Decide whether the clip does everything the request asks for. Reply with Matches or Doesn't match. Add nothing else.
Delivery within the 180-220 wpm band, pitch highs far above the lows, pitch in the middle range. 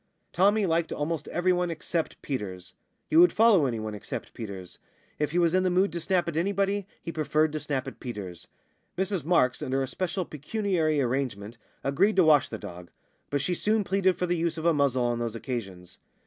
Matches